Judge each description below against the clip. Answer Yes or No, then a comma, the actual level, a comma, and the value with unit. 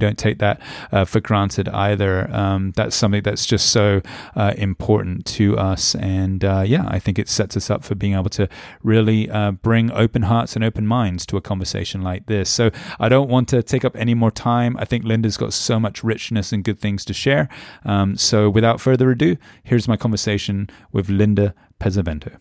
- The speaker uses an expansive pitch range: No, narrow, 2.6 semitones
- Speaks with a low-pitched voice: Yes, low, 105 Hz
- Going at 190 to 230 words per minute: Yes, fast, 205 wpm